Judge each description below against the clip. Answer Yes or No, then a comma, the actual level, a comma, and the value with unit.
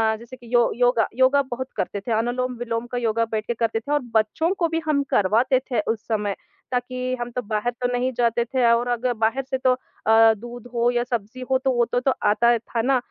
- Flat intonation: Yes, narrow, 1.8 semitones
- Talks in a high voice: Yes, high, 240 Hz